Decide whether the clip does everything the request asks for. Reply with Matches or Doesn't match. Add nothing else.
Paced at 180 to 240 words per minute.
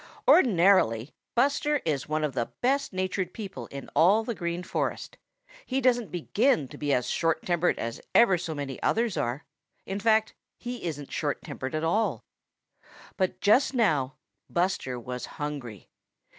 Doesn't match